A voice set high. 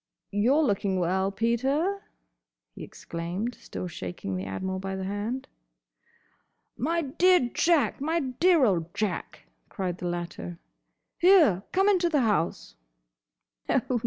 Yes: high, 215 Hz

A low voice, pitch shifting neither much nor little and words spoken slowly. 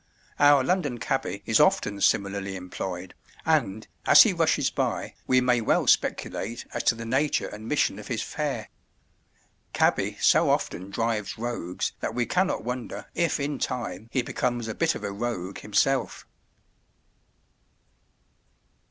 No: low, 115 Hz; average, 4.4 semitones; average, 145 wpm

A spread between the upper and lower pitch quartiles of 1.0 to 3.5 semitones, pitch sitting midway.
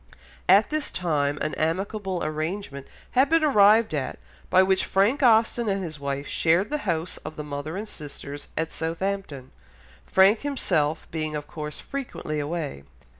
No: average, 5.3 semitones; medium, 170 Hz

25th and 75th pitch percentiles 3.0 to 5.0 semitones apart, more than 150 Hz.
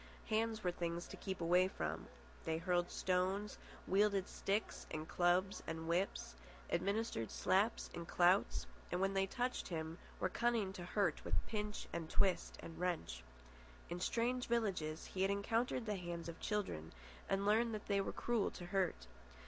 Yes: average, 3.4 semitones; high, 190 Hz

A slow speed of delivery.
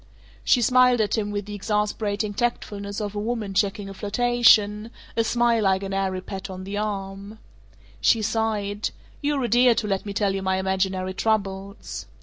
No: average, 175 wpm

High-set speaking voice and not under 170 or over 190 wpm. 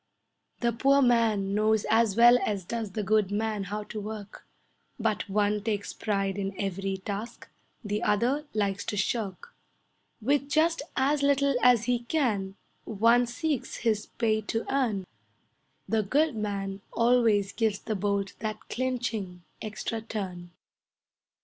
No: high, 215 Hz; average, 140 wpm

